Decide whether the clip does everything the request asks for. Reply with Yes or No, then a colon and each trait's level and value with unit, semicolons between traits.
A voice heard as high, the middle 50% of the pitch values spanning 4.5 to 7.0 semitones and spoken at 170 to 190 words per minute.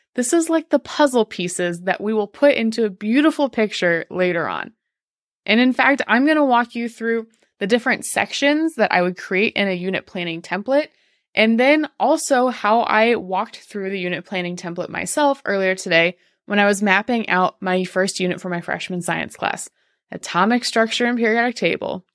Yes: high, 215 Hz; average, 5.2 semitones; average, 185 wpm